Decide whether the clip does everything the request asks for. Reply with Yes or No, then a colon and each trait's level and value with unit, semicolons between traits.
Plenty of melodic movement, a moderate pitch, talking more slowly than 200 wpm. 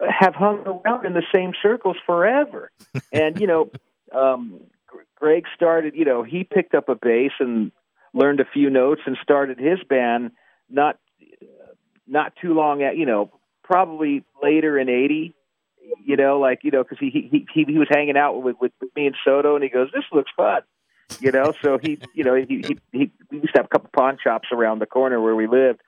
No: wide, 6.0 semitones; medium, 150 Hz; fast, 205 wpm